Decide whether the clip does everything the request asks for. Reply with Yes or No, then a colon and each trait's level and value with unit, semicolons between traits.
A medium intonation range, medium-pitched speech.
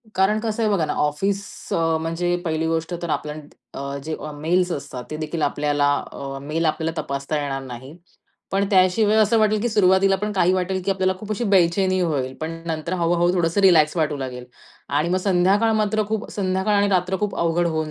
Yes: average, 4.0 semitones; medium, 175 Hz